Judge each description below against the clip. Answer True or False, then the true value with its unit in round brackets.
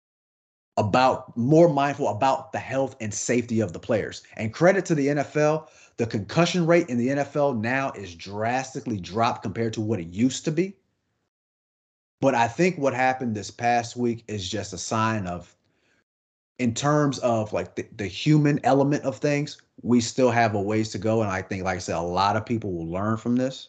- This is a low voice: True (120 Hz)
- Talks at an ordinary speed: True (195 wpm)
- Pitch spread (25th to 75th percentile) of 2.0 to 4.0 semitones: False (4.7 semitones)